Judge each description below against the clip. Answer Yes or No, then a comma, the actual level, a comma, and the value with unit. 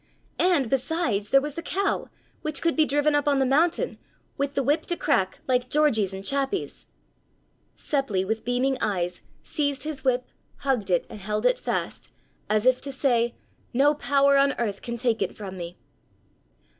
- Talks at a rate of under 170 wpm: No, average, 175 wpm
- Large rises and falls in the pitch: No, average, 4.9 semitones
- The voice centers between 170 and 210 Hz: No, very high, 270 Hz